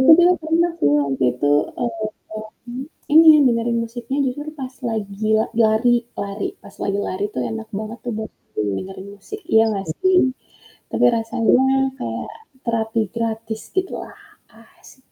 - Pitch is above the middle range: Yes, high, 225 Hz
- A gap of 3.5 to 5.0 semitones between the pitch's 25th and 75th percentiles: Yes, average, 4.5 semitones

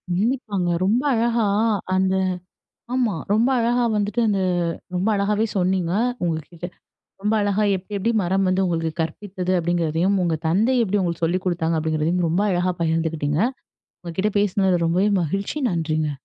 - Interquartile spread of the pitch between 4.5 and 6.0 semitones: No, average, 3.8 semitones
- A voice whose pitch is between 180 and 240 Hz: Yes, medium, 185 Hz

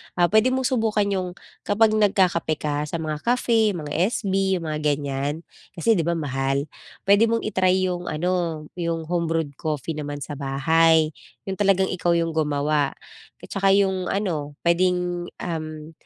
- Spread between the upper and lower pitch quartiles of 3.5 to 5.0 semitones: Yes, average, 4.1 semitones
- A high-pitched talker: No, medium, 170 Hz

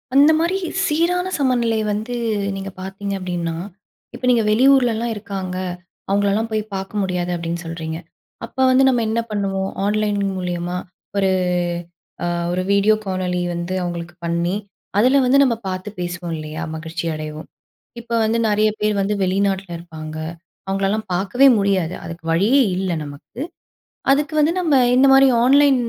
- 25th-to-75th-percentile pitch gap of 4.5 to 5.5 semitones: Yes, average, 4.9 semitones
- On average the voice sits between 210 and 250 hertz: No, high, 195 Hz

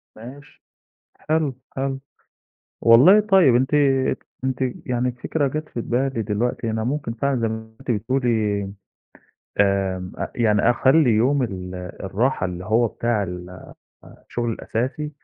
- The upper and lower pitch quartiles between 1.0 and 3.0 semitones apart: No, average, 4.0 semitones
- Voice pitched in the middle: No, low, 120 Hz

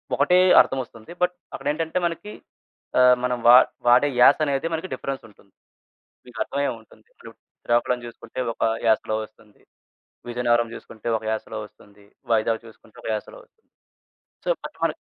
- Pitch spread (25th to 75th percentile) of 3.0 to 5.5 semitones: Yes, average, 4.2 semitones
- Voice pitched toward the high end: No, low, 120 Hz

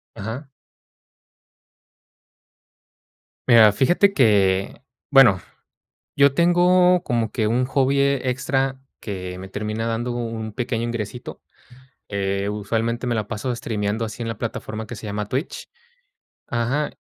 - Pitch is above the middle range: No, low, 115 Hz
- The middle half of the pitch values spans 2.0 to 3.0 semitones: No, average, 4.0 semitones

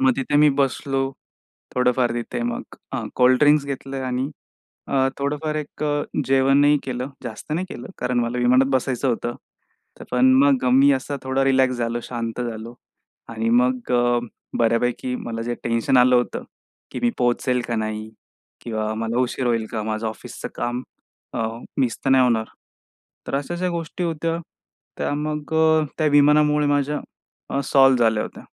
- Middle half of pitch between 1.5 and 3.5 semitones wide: Yes, average, 3.0 semitones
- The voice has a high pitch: No, low, 130 Hz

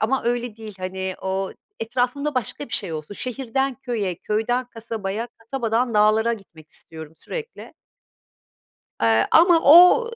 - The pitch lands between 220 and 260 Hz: Yes, high, 225 Hz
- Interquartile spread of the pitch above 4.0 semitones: Yes, average, 4.8 semitones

